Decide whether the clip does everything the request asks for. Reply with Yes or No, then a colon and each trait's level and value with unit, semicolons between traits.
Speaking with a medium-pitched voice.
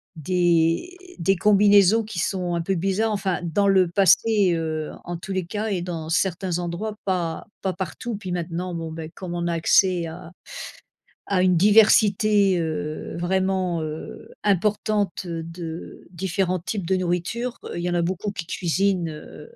Yes: medium, 180 Hz